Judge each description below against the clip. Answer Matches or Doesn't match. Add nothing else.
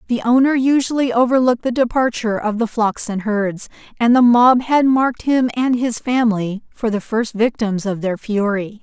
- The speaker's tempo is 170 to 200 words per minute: Matches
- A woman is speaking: Matches